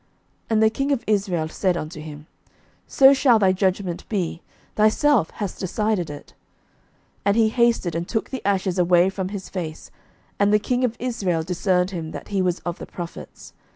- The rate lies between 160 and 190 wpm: Yes, average, 185 wpm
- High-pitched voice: Yes, high, 195 Hz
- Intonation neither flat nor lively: Yes, average, 4.0 semitones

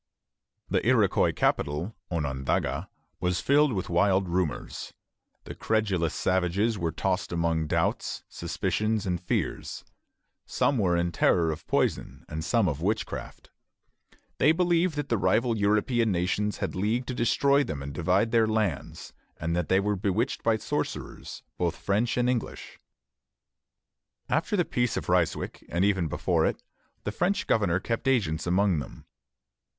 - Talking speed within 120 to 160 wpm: Yes, average, 145 wpm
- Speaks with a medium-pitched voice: No, low, 100 Hz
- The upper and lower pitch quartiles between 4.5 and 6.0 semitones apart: Yes, average, 5.1 semitones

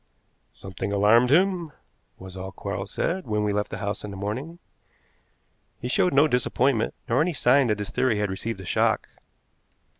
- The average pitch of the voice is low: Yes, low, 110 Hz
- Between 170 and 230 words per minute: Yes, average, 175 wpm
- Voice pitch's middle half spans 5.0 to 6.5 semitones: Yes, average, 5.3 semitones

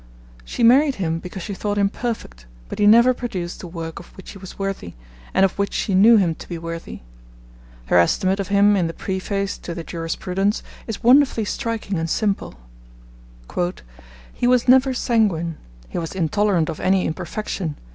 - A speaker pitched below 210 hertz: Yes, high, 190 Hz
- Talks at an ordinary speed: Yes, average, 175 wpm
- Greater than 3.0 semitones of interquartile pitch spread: Yes, average, 4.2 semitones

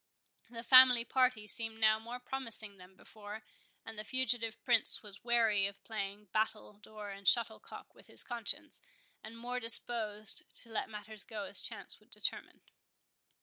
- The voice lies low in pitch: No, high, 220 Hz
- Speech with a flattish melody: Yes, narrow, 2.1 semitones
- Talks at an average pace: Yes, average, 150 wpm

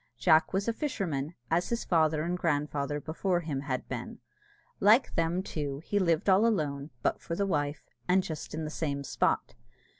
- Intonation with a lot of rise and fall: No, average, 4.2 semitones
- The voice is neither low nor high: Yes, medium, 160 Hz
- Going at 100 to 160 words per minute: No, average, 180 wpm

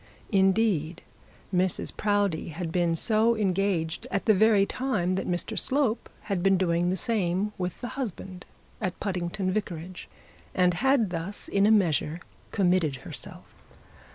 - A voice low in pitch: No, high, 190 Hz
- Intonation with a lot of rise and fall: No, average, 3.3 semitones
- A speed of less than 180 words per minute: Yes, average, 140 wpm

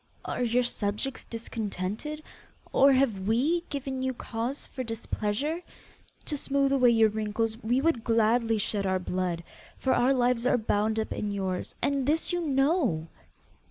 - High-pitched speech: Yes, high, 235 Hz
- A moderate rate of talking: Yes, average, 155 wpm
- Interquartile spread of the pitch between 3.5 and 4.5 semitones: Yes, average, 4.2 semitones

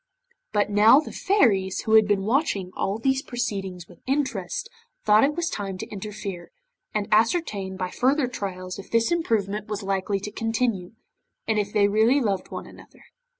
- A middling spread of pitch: Yes, average, 3.7 semitones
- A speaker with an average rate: Yes, average, 170 wpm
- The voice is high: Yes, high, 210 Hz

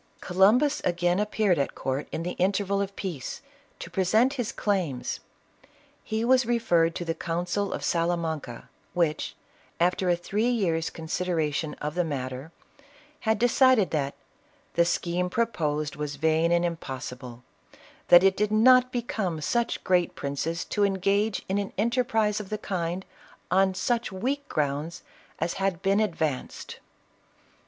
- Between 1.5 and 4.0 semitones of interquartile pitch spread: No, average, 4.5 semitones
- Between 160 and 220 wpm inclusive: No, average, 150 wpm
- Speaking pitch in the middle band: Yes, medium, 180 Hz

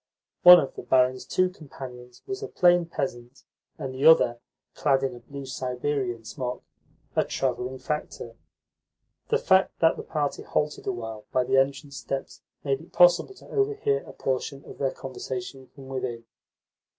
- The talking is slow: No, average, 160 wpm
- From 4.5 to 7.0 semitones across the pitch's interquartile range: No, average, 3.5 semitones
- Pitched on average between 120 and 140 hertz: Yes, low, 135 Hz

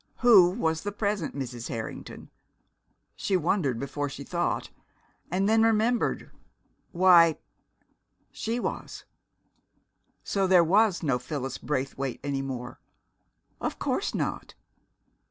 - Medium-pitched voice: Yes, medium, 170 Hz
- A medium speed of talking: No, slow, 110 wpm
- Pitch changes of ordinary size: No, wide, 6.7 semitones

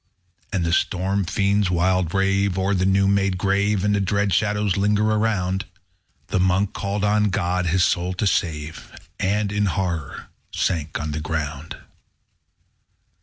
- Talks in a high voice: No, very low, 95 Hz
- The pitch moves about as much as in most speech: No, narrow, 2.2 semitones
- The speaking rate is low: No, average, 145 wpm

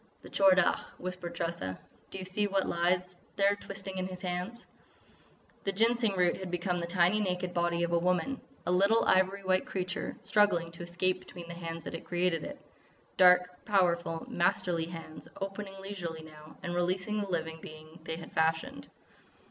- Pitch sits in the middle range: Yes, medium, 180 Hz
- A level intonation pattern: Yes, narrow, 2.1 semitones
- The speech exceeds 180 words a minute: No, average, 170 wpm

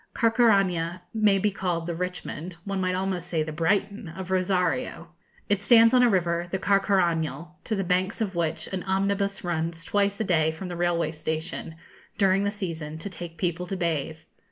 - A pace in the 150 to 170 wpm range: No, average, 180 wpm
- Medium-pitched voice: Yes, medium, 180 Hz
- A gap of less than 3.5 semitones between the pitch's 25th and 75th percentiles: Yes, average, 2.9 semitones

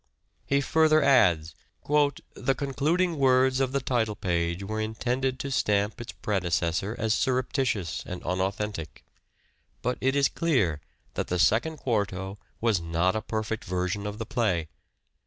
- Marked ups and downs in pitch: Yes, wide, 6.2 semitones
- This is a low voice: Yes, low, 110 Hz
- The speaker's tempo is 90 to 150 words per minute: Yes, average, 145 wpm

